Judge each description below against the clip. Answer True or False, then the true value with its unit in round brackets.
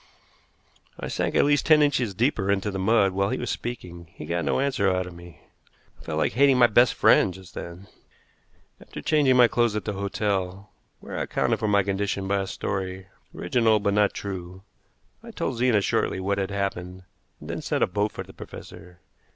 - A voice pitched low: True (100 Hz)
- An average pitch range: True (3.7 semitones)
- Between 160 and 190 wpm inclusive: False (200 wpm)